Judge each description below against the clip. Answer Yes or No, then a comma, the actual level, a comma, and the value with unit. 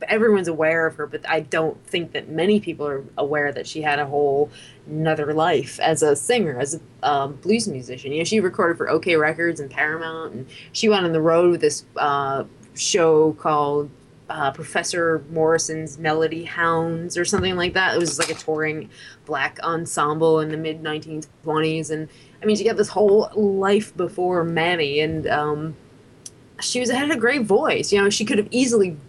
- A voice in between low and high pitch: Yes, medium, 160 Hz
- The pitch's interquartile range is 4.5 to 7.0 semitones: No, average, 2.9 semitones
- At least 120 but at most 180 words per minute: No, average, 190 wpm